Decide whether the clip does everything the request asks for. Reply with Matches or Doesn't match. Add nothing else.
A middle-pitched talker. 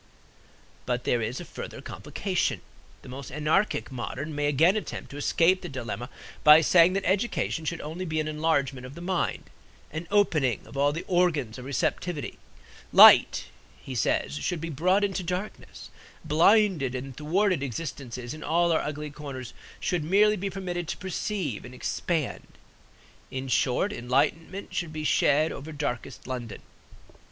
Matches